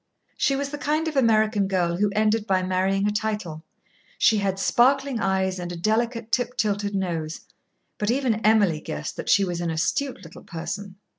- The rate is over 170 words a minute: Yes, average, 180 wpm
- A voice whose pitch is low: No, high, 205 Hz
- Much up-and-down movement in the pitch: No, average, 3.8 semitones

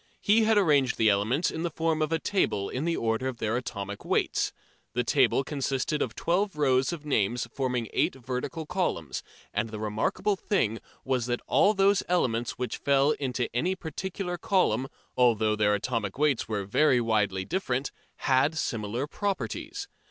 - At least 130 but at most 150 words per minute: No, average, 165 wpm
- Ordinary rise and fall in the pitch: No, wide, 6.5 semitones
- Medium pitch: No, low, 130 Hz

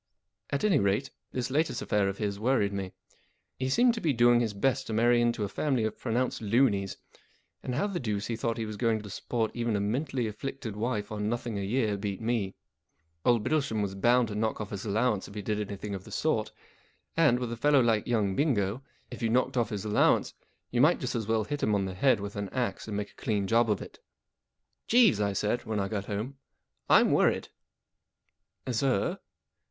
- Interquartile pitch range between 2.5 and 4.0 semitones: Yes, average, 3.5 semitones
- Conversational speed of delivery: No, fast, 220 wpm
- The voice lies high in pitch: No, low, 110 Hz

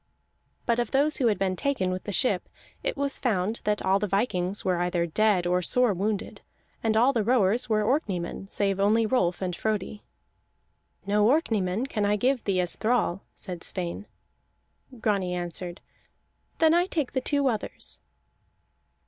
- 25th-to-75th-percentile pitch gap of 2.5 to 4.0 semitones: No, average, 4.8 semitones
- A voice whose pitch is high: Yes, high, 210 Hz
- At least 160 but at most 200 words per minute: Yes, average, 165 wpm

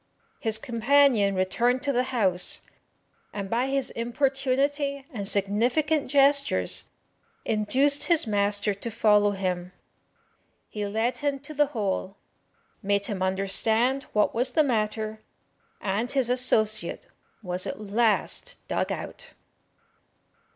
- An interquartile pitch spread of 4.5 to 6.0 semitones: Yes, average, 5.1 semitones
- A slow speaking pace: Yes, slow, 115 wpm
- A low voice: No, high, 230 Hz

